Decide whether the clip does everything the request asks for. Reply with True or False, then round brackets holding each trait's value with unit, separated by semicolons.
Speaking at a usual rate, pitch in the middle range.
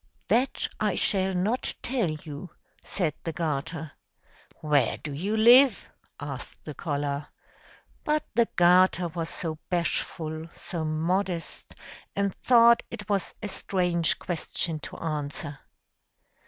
False (120 wpm; 170 Hz)